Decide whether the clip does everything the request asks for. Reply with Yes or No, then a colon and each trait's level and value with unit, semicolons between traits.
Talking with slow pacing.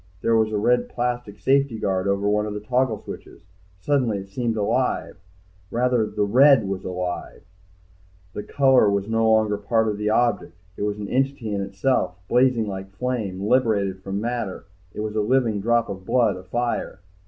No: average, 175 wpm